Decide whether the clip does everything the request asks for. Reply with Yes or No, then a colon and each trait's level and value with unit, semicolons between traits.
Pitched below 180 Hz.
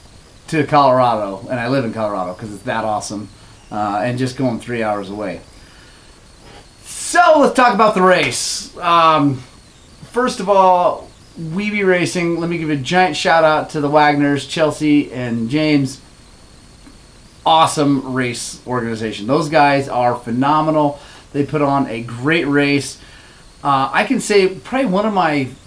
Yes: medium, 140 Hz